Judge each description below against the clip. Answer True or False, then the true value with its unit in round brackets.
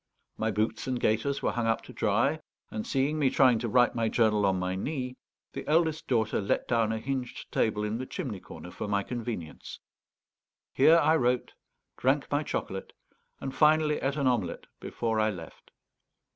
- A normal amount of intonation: True (4.1 semitones)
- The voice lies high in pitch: False (120 Hz)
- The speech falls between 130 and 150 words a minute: False (180 wpm)